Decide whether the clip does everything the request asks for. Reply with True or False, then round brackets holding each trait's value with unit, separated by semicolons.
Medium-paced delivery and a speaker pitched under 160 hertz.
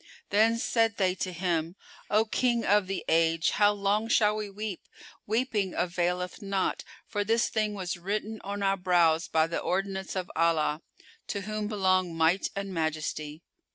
False (160 wpm; 195 Hz)